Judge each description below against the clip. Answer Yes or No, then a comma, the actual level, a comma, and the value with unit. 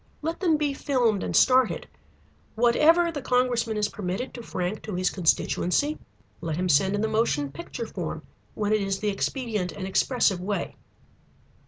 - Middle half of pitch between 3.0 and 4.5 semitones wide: No, average, 5.2 semitones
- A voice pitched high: Yes, high, 215 Hz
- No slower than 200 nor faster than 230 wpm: No, average, 165 wpm